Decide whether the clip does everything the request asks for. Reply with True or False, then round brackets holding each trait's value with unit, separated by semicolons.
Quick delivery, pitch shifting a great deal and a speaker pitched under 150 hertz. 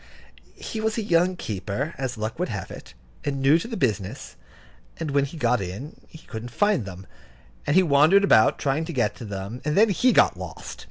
True (210 wpm; 8.1 semitones; 140 Hz)